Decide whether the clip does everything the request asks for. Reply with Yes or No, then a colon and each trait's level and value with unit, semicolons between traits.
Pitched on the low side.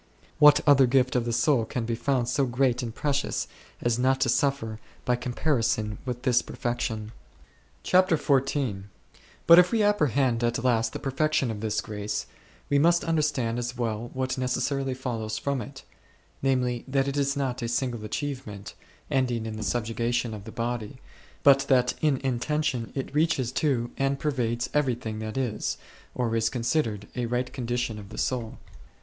Yes: low, 125 Hz